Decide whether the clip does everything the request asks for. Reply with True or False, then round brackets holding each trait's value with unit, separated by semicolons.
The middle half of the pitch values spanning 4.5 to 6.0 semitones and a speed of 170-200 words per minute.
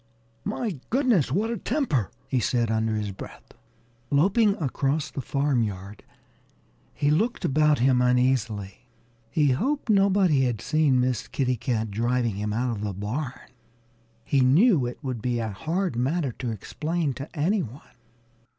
False (5.5 semitones; 150 wpm)